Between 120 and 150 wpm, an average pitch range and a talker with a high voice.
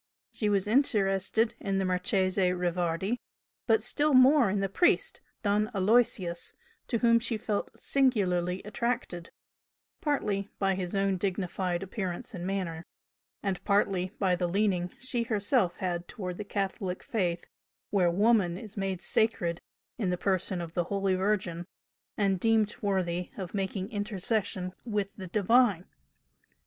Yes: average, 140 wpm; average, 3.0 semitones; high, 195 Hz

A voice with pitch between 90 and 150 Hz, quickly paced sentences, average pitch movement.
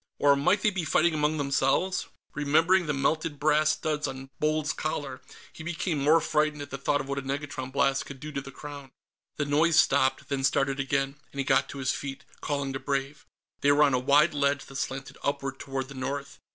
No: medium, 140 Hz; fast, 215 wpm; narrow, 1.9 semitones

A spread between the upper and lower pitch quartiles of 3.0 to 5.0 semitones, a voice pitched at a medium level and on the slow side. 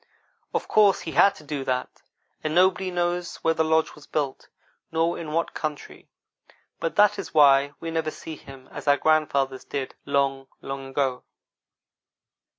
No: average, 3.3 semitones; medium, 155 Hz; average, 155 wpm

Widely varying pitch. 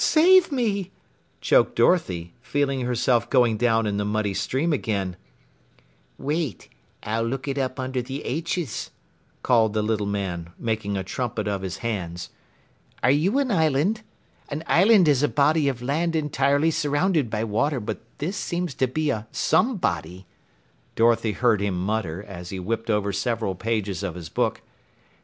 Yes: wide, 6.4 semitones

